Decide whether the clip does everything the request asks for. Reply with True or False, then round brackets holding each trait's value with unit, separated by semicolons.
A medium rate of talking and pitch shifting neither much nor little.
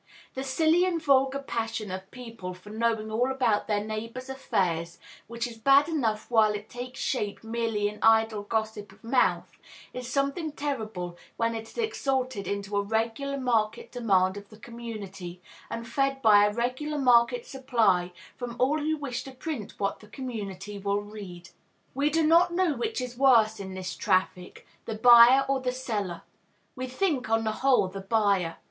True (175 wpm; 4.4 semitones)